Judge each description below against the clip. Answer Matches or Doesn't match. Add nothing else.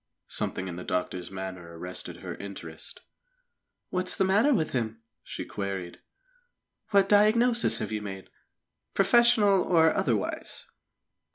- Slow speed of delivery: Matches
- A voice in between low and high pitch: Doesn't match